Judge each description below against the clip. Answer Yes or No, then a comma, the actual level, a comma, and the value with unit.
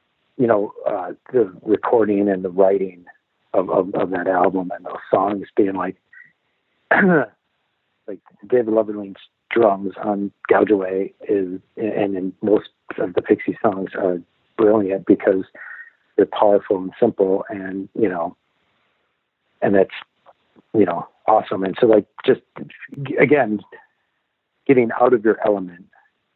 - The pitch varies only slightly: Yes, narrow, 2.0 semitones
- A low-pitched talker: Yes, low, 100 Hz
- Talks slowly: Yes, slow, 130 wpm